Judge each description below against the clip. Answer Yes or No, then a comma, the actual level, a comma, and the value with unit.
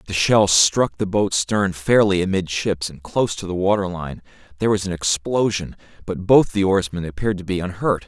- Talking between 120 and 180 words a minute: No, average, 195 wpm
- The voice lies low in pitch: Yes, very low, 95 Hz